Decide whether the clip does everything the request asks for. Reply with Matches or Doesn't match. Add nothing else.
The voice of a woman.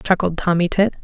Matches